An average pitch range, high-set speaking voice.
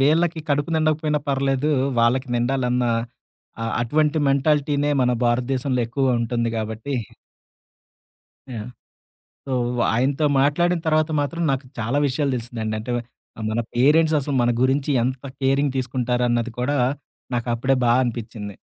No: average, 3.3 semitones; low, 130 Hz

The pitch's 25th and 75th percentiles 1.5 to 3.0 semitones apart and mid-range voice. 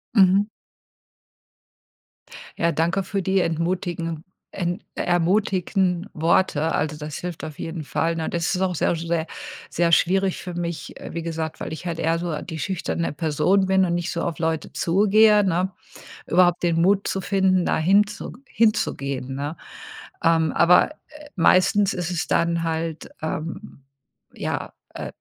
Yes: narrow, 2.6 semitones; medium, 170 Hz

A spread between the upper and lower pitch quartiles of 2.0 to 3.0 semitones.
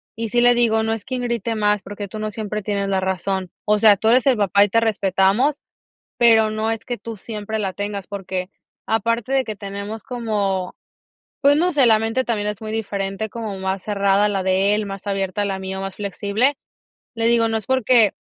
Yes: narrow, 2.5 semitones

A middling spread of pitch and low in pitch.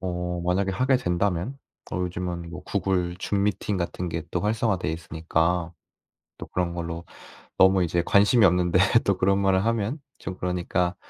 No: narrow, 2.3 semitones; very low, 90 Hz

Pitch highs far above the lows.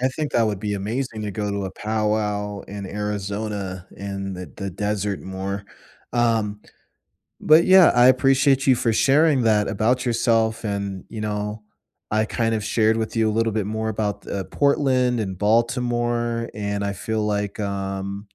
No: average, 2.7 semitones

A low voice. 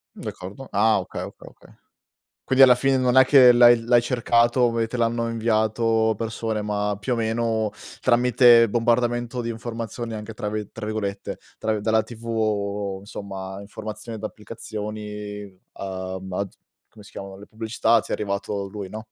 Yes: low, 110 Hz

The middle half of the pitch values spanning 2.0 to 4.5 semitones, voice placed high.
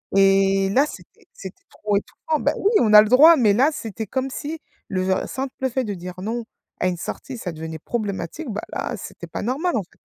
No: wide, 5.5 semitones; high, 215 Hz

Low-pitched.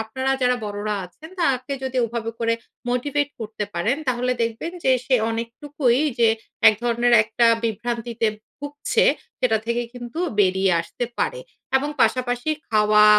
No: high, 240 Hz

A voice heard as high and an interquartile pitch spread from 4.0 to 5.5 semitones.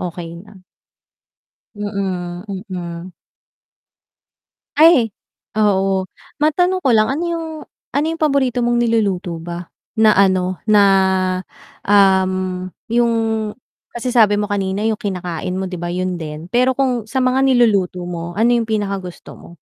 Yes: high, 205 Hz; average, 4.7 semitones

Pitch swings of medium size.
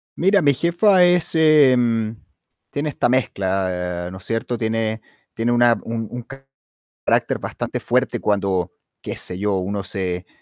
No: wide, 6.4 semitones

